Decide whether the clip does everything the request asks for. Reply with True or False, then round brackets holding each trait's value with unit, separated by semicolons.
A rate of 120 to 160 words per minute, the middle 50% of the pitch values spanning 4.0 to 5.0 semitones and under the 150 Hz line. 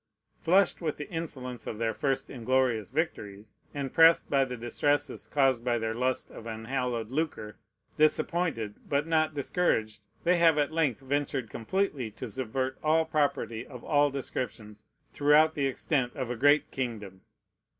True (150 wpm; 4.6 semitones; 135 Hz)